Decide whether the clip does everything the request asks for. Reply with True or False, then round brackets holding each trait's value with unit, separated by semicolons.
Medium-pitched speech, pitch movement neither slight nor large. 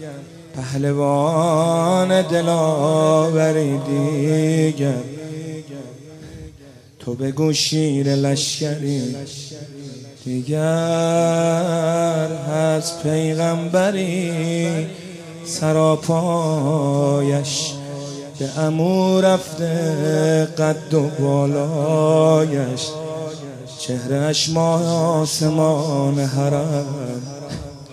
False (155 Hz; 2.3 semitones)